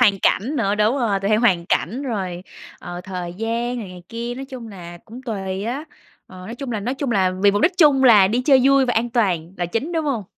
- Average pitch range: Yes, average, 4.8 semitones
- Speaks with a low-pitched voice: No, high, 225 Hz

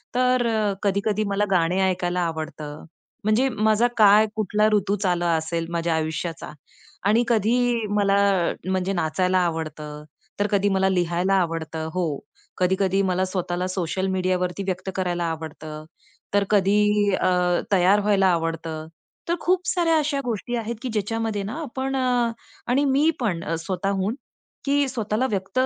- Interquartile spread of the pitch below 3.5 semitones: No, average, 3.8 semitones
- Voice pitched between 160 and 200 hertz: Yes, high, 195 Hz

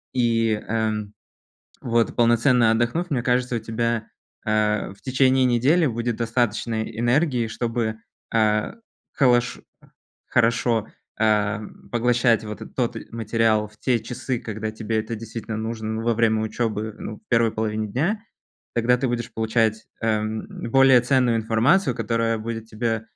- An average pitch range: No, narrow, 1.8 semitones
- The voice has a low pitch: Yes, low, 115 Hz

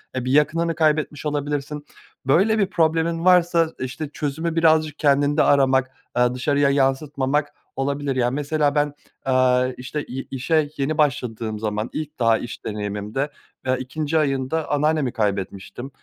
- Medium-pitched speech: Yes, medium, 145 Hz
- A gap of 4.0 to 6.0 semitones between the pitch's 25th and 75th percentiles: No, average, 3.2 semitones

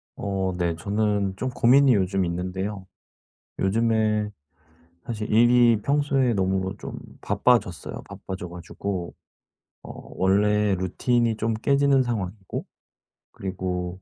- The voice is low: Yes, low, 105 Hz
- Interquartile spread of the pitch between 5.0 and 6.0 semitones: No, average, 3.8 semitones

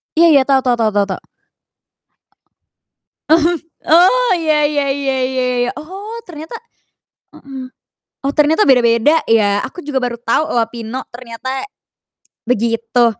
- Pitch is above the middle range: Yes, very high, 265 Hz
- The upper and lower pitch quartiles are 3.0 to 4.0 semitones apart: No, average, 4.7 semitones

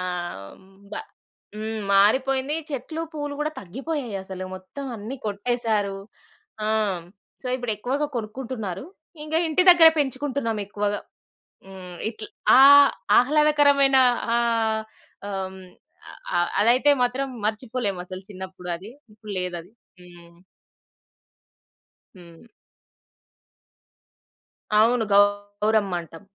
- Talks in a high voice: Yes, high, 220 Hz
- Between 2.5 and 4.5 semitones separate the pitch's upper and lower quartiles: No, wide, 5.5 semitones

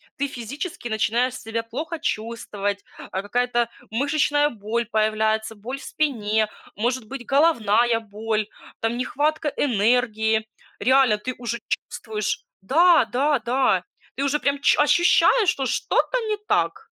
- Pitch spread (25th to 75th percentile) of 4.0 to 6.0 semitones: Yes, average, 4.4 semitones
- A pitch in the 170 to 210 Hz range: No, high, 240 Hz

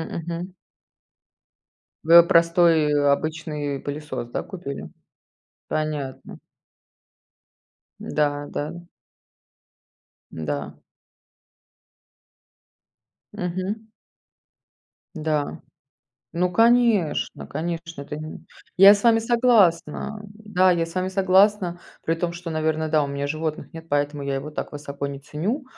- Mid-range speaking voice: Yes, medium, 165 Hz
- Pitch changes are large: No, average, 3.8 semitones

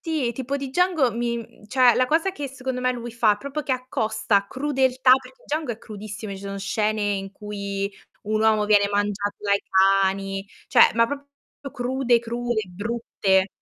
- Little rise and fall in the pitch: No, average, 4.1 semitones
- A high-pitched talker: Yes, high, 235 Hz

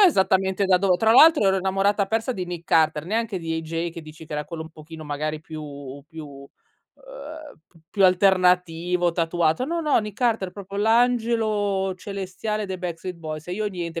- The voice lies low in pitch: No, medium, 180 Hz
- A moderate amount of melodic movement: Yes, average, 4.0 semitones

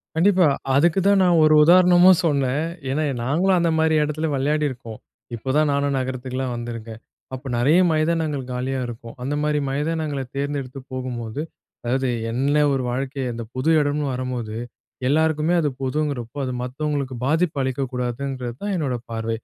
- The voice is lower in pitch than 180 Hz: Yes, medium, 140 Hz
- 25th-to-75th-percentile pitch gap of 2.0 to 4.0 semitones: Yes, average, 3.4 semitones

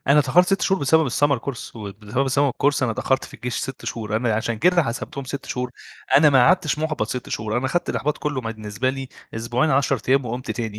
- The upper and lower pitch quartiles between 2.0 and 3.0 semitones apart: No, average, 3.9 semitones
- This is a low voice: Yes, low, 130 Hz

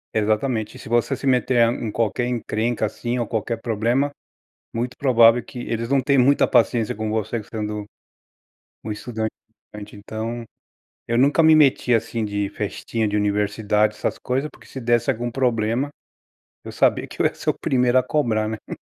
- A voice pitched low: Yes, low, 115 Hz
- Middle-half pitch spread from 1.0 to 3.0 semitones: Yes, narrow, 2.5 semitones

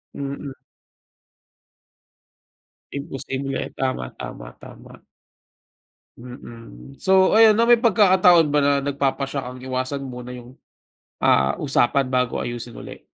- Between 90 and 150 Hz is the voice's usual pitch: Yes, low, 135 Hz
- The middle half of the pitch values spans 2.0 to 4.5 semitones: Yes, average, 2.9 semitones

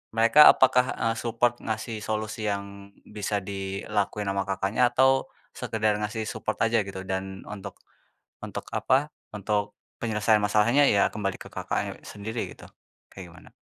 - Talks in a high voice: No, low, 105 Hz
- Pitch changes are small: Yes, narrow, 2.3 semitones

